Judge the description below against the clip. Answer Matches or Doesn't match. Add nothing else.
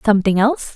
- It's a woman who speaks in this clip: Matches